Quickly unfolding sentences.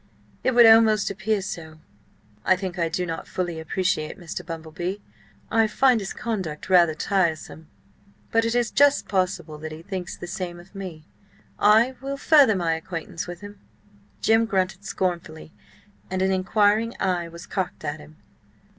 No: average, 165 wpm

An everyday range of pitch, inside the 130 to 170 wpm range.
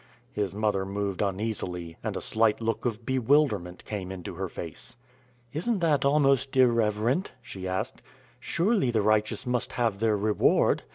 Yes: average, 4.5 semitones; average, 150 wpm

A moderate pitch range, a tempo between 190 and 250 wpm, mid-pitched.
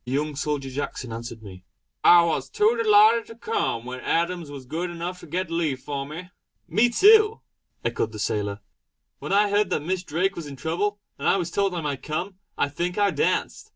No: wide, 6.1 semitones; fast, 205 wpm; medium, 170 Hz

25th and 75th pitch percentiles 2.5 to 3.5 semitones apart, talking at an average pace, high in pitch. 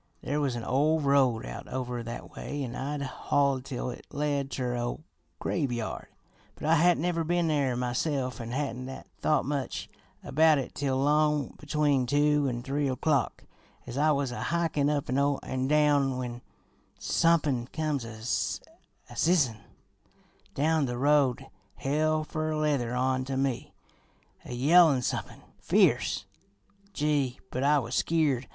No: average, 2.9 semitones; average, 145 wpm; medium, 140 Hz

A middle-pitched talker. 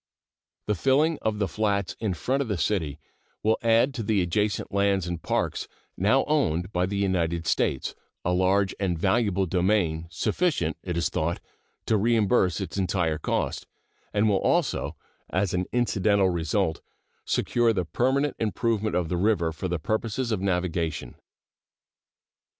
No: low, 100 Hz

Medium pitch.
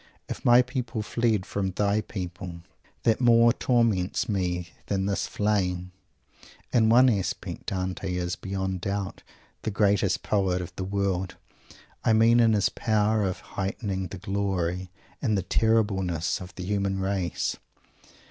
No: low, 100 Hz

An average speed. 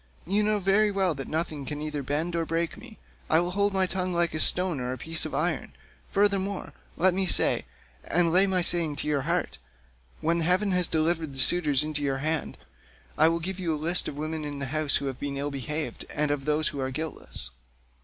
No: fast, 225 wpm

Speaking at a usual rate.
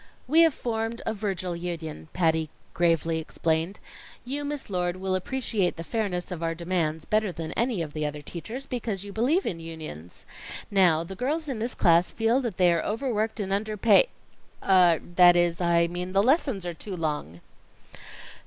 Yes: average, 175 wpm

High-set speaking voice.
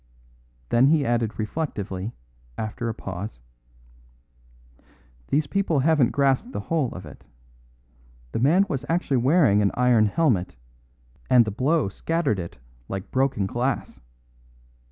No: low, 125 Hz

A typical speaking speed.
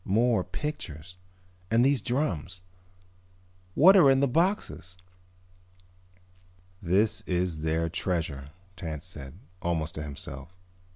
No: slow, 105 wpm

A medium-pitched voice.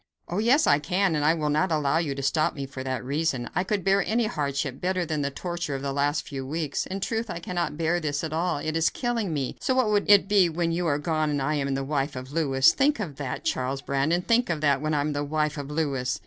Yes: medium, 155 Hz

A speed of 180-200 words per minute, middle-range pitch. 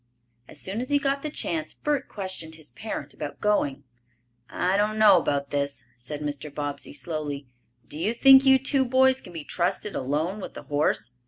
Yes: average, 185 wpm; medium, 180 Hz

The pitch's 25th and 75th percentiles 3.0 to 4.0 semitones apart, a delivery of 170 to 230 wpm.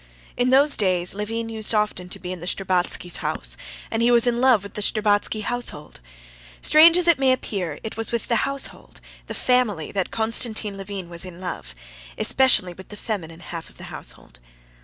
No: average, 4.8 semitones; average, 190 wpm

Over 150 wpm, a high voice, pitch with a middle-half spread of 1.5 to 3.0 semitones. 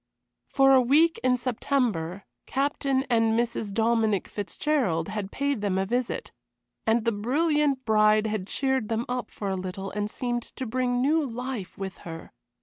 No: average, 160 wpm; high, 235 Hz; average, 4.2 semitones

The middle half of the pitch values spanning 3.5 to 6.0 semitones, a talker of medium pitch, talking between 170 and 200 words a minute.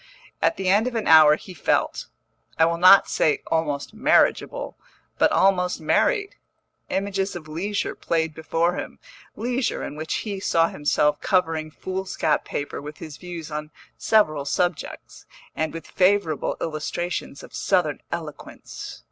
No: average, 3.9 semitones; medium, 170 Hz; average, 140 wpm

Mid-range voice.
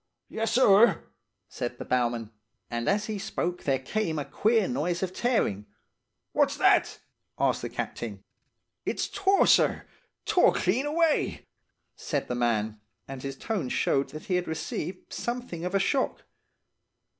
Yes: medium, 180 Hz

